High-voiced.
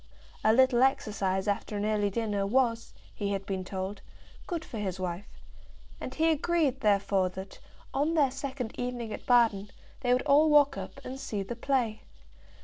Yes: high, 230 Hz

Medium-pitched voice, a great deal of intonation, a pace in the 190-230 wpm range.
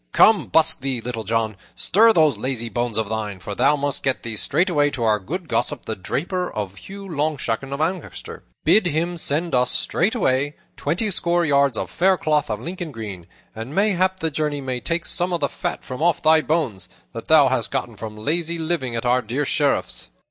Yes: medium, 145 Hz; wide, 6.4 semitones; average, 195 wpm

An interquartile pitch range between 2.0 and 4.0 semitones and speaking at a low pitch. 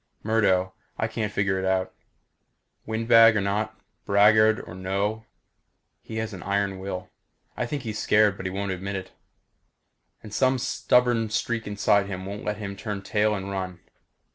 Yes: narrow, 2.4 semitones; low, 105 Hz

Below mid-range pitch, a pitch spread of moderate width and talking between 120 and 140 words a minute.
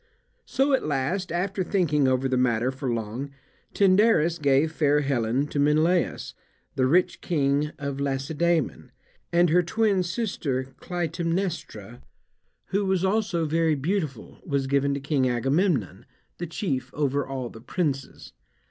No: medium, 150 Hz; average, 4.7 semitones; slow, 135 wpm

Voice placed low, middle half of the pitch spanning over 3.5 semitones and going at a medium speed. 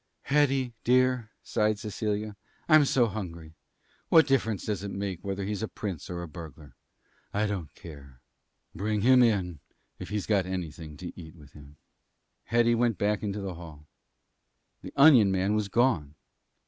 Yes: low, 100 Hz; average, 5.0 semitones; average, 160 wpm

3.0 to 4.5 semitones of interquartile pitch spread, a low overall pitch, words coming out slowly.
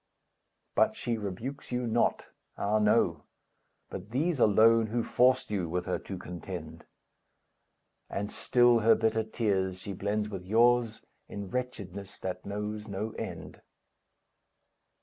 Yes: average, 3.3 semitones; low, 105 Hz; slow, 130 wpm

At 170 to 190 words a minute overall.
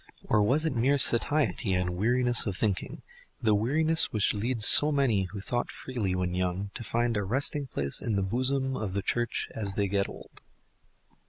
Yes: average, 180 wpm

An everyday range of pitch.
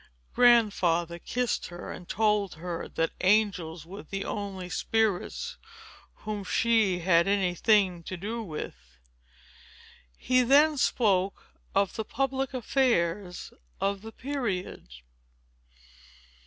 Yes: average, 4.4 semitones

